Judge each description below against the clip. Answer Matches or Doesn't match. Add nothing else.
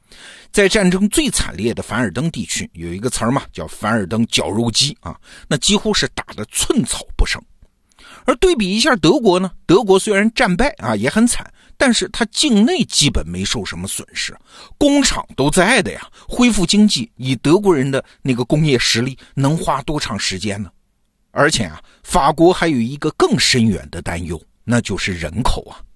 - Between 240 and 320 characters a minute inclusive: Matches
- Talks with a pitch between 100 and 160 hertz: Matches